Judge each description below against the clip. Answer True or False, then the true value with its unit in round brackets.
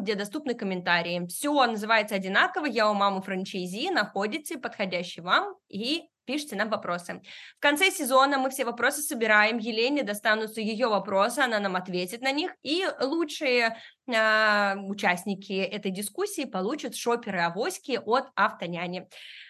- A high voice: True (220 Hz)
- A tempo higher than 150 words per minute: False (135 wpm)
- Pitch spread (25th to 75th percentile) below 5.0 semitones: False (5.3 semitones)